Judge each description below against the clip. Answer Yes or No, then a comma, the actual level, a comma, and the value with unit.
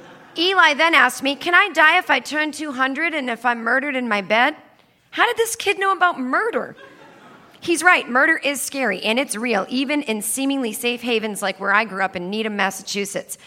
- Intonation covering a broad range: Yes, wide, 6.5 semitones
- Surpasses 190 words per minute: Yes, fast, 205 wpm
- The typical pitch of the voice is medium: No, very high, 265 Hz